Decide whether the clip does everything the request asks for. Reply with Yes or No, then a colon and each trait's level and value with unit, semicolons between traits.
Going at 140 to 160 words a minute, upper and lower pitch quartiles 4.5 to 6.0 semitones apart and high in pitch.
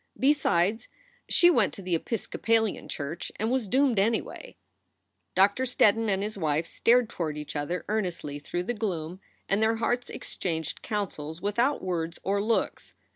Yes: average, 150 wpm; average, 5.1 semitones; high, 200 Hz